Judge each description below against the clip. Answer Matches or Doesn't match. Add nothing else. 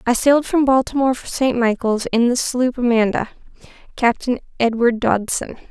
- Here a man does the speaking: Doesn't match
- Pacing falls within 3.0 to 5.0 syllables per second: Doesn't match